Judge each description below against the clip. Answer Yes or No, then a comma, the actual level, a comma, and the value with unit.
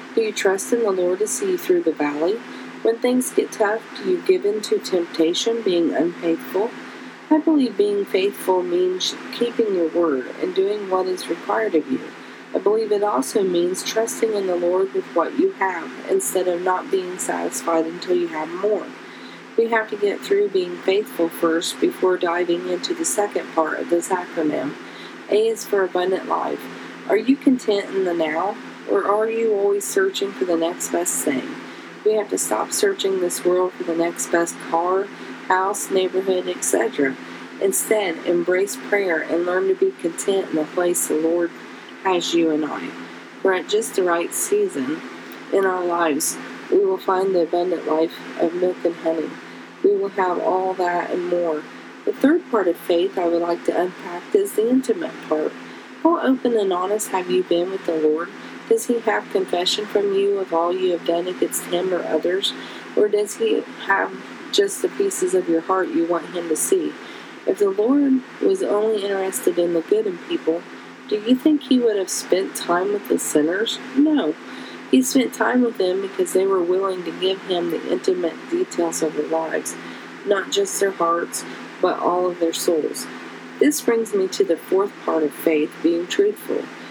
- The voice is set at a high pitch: Yes, high, 195 Hz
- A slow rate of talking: No, average, 190 wpm